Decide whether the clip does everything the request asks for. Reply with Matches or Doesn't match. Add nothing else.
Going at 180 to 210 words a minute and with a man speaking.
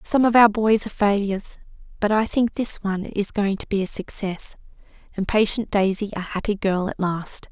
Doesn't match